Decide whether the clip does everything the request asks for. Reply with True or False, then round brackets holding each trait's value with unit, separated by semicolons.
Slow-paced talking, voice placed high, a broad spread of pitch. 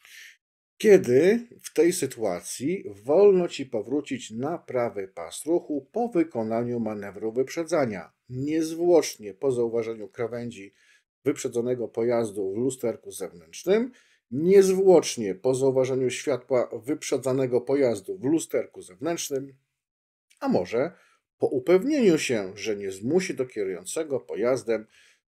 False (105 wpm; 135 Hz; 8.1 semitones)